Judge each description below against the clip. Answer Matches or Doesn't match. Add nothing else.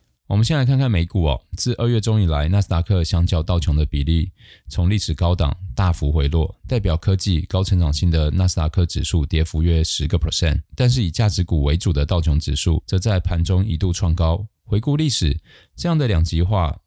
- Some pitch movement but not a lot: Matches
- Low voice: Matches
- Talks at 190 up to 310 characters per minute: Doesn't match